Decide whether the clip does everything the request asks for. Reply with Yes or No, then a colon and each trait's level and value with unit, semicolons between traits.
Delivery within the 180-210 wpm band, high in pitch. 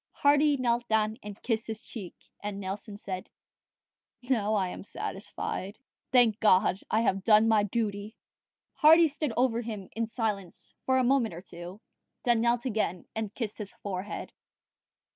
No: average, 155 wpm; high, 220 Hz